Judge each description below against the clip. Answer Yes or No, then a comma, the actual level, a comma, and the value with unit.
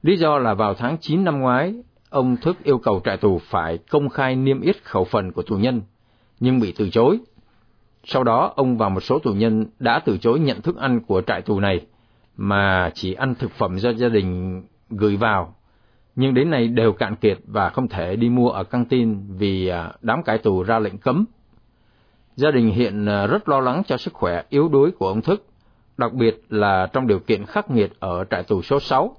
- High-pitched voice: No, low, 115 Hz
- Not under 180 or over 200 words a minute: No, average, 215 wpm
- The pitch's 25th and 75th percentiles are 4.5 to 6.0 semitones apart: No, average, 4.1 semitones